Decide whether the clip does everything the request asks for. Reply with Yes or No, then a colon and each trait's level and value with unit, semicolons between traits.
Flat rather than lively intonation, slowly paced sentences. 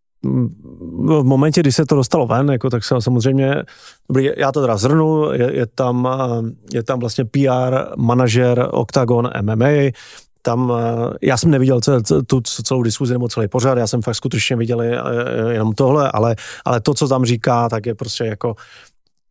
No: narrow, 2.2 semitones; average, 165 wpm